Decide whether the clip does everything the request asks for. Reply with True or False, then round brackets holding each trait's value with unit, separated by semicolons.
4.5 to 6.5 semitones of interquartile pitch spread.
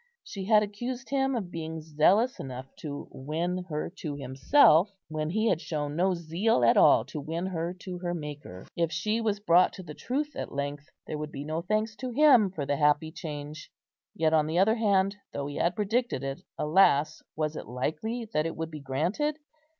True (5.6 semitones)